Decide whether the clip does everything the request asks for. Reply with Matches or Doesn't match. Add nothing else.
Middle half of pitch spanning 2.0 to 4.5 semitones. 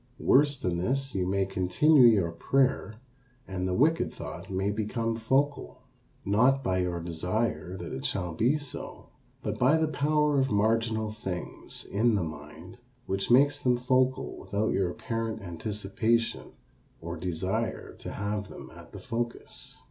Doesn't match